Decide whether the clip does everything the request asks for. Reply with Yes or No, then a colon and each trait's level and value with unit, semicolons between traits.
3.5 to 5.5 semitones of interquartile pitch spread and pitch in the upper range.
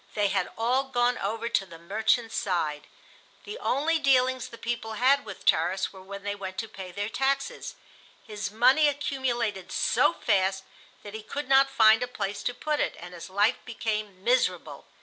Yes: average, 4.8 semitones; high, 220 Hz